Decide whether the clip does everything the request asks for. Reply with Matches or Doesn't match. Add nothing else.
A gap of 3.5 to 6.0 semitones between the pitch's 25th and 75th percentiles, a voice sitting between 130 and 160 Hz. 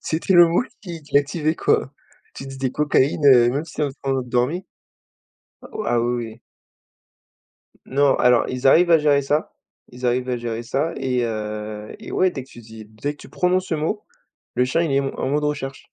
Matches